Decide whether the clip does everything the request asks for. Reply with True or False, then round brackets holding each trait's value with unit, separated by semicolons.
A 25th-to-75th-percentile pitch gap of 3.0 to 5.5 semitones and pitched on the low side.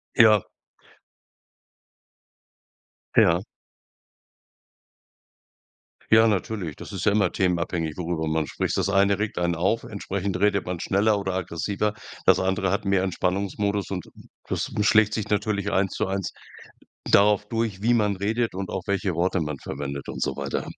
False (2.5 semitones; 100 Hz)